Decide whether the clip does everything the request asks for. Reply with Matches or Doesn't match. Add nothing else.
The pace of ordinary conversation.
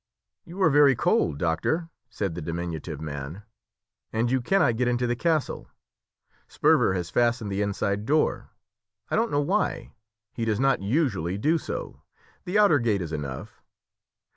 Matches